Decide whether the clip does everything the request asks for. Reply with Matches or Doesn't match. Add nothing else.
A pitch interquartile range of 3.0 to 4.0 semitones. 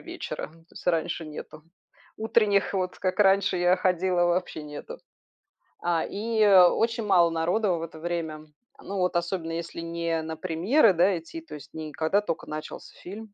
Matches